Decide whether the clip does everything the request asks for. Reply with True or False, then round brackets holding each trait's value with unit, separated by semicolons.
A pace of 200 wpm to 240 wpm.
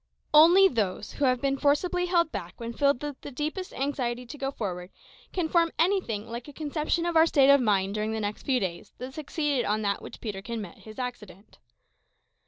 True (205 wpm)